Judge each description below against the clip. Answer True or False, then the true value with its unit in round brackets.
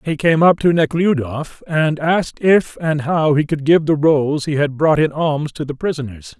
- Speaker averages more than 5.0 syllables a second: False (4.5 syllables/s)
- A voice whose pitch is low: False (150 Hz)